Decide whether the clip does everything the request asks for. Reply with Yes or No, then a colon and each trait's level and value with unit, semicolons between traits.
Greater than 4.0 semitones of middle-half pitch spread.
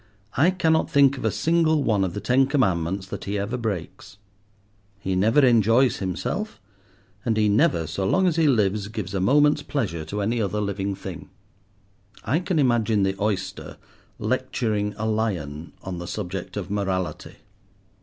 Yes: average, 5.2 semitones